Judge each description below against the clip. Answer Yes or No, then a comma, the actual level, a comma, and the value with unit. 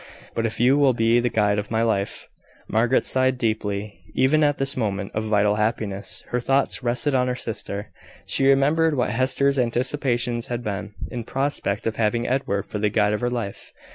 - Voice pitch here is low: Yes, low, 120 Hz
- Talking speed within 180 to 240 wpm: Yes, average, 195 wpm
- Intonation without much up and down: No, average, 3.6 semitones